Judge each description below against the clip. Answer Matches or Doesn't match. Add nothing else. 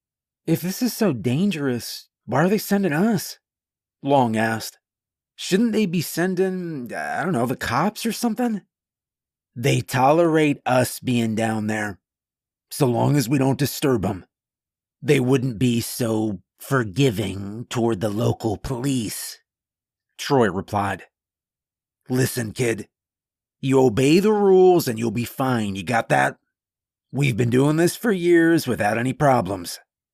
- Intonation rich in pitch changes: Matches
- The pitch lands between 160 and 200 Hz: Doesn't match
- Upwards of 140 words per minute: Doesn't match